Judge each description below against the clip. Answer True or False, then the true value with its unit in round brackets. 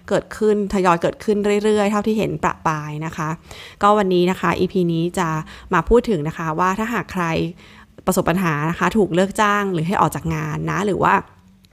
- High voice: False (180 Hz)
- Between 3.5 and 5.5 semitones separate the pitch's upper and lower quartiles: True (4.1 semitones)